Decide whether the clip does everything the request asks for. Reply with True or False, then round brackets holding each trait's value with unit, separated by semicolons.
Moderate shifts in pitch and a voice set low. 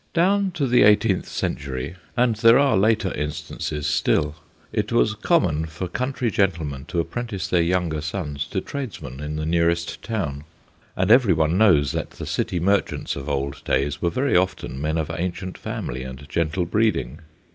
False (6.0 semitones; 85 Hz)